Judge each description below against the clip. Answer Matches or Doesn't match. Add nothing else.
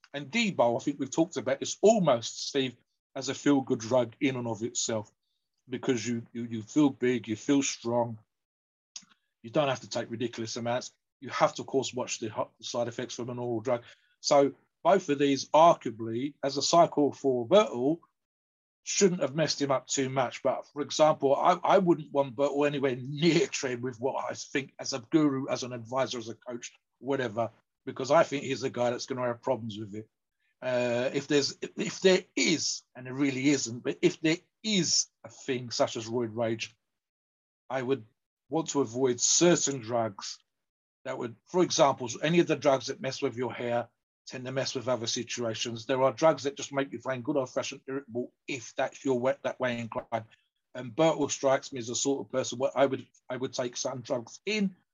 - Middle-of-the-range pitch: Doesn't match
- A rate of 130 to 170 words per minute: Doesn't match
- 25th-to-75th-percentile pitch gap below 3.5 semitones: Matches